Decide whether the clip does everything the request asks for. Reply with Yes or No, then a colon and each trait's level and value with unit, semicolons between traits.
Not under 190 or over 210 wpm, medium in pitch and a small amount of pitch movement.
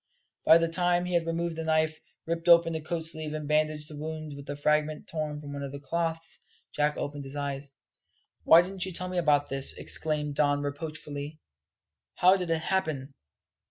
Yes: average, 195 wpm; medium, 155 Hz; narrow, 2.3 semitones